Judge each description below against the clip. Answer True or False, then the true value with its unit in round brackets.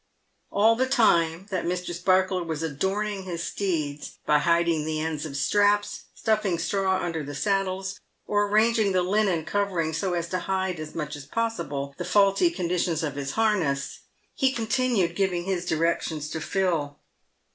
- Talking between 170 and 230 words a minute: False (160 wpm)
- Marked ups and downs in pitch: False (4.0 semitones)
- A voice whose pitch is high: False (180 Hz)